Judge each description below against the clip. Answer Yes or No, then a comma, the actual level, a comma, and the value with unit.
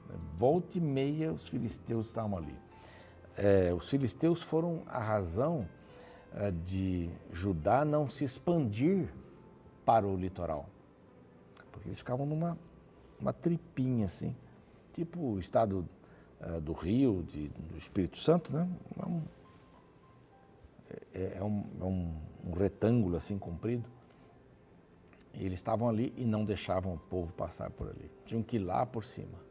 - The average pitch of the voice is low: Yes, low, 110 Hz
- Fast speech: No, average, 135 wpm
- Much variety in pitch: Yes, wide, 7.2 semitones